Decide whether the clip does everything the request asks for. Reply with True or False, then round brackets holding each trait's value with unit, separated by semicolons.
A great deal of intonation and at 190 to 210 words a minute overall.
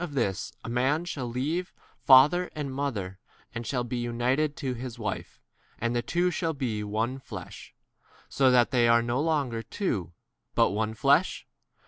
False (3.6 semitones; 195 wpm)